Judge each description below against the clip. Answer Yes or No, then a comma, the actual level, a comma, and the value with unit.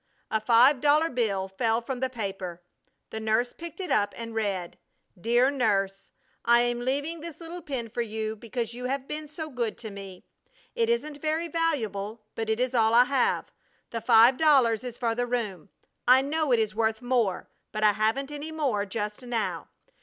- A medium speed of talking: Yes, average, 190 wpm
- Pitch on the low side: No, high, 240 Hz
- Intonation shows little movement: No, average, 4.2 semitones